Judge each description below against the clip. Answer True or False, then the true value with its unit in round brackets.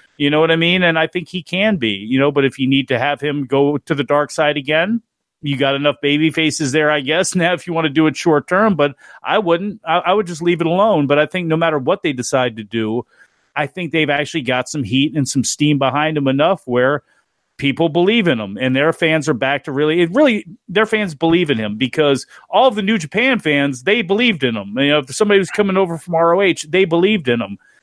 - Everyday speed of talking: False (255 wpm)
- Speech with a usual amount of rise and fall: True (3.8 semitones)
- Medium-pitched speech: True (155 Hz)